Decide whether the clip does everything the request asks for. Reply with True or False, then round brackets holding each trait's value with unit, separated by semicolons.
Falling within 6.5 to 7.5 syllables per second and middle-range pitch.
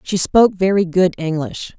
False (4.9 syllables/s; 180 Hz)